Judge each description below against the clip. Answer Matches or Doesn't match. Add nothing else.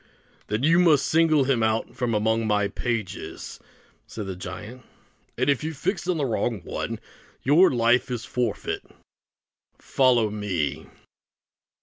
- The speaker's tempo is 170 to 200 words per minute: Doesn't match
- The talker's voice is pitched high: Doesn't match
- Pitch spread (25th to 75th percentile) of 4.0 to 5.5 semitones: Matches